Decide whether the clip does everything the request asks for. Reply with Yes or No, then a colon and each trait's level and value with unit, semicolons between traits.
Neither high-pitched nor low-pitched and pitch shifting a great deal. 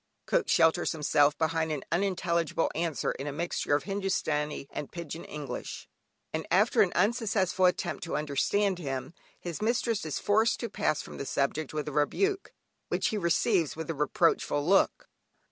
No: medium, 165 Hz; average, 4.7 semitones